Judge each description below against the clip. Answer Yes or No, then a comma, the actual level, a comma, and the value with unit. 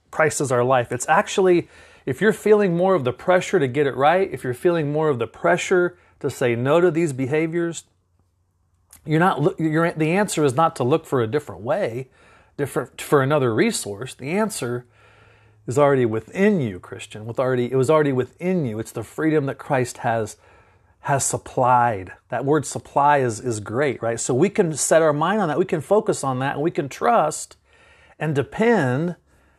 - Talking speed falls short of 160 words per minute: No, average, 195 wpm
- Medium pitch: Yes, medium, 145 Hz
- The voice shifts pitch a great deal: Yes, wide, 6.0 semitones